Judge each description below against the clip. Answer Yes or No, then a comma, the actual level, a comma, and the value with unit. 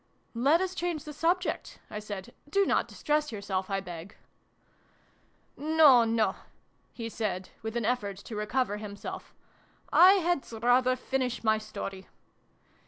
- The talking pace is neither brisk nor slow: Yes, average, 165 wpm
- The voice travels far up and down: Yes, wide, 6.3 semitones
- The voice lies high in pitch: Yes, high, 235 Hz